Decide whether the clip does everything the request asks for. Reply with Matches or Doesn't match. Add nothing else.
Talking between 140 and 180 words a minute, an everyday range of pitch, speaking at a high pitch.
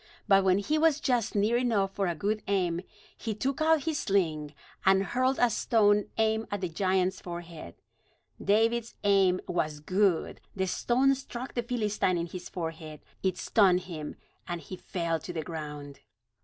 Matches